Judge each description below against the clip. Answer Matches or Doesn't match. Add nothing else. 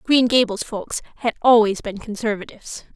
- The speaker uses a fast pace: Doesn't match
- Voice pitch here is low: Doesn't match